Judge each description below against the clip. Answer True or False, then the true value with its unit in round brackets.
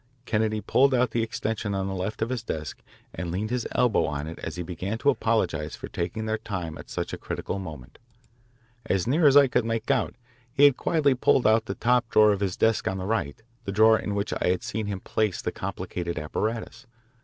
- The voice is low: True (110 Hz)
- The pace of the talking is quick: True (225 wpm)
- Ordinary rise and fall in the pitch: True (3.8 semitones)